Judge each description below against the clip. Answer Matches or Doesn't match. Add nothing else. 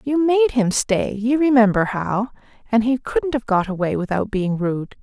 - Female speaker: Matches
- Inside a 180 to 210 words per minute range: Doesn't match